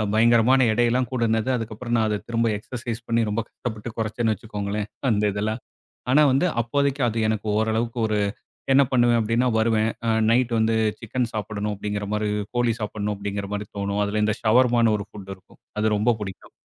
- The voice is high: No, low, 110 Hz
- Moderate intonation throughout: No, narrow, 2.2 semitones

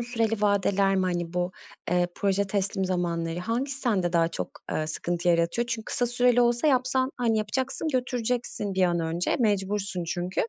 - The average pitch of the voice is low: No, high, 200 Hz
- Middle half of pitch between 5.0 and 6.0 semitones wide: Yes, average, 5.3 semitones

